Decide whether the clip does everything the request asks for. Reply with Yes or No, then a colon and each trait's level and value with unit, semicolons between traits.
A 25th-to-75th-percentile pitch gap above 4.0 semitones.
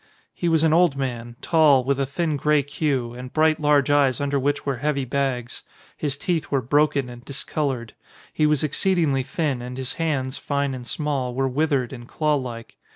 No: average, 2.8 semitones